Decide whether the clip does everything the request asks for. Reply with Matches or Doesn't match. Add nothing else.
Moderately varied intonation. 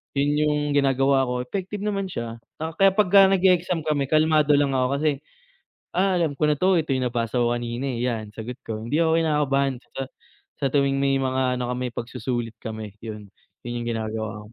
Matches